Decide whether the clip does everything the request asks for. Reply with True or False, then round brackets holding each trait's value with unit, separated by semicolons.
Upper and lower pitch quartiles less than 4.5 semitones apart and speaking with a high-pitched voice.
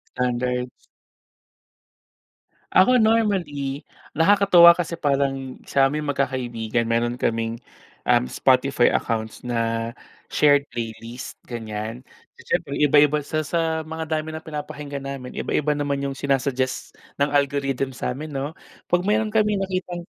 False (4.1 semitones; 140 Hz)